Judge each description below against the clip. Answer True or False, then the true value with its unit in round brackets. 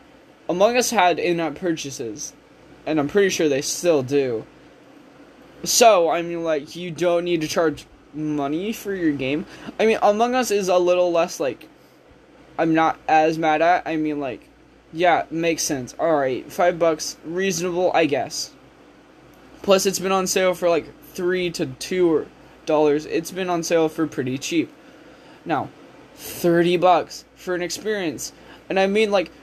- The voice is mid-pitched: True (170 Hz)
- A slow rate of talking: False (160 wpm)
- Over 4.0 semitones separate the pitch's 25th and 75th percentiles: False (3.3 semitones)